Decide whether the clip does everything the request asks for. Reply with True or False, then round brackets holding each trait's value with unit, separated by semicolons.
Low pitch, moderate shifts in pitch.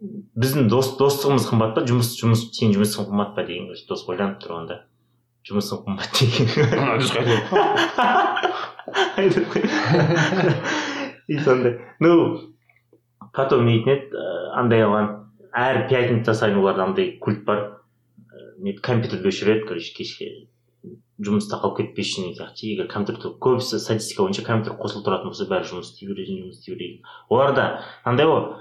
False (125 Hz; 7.3 semitones)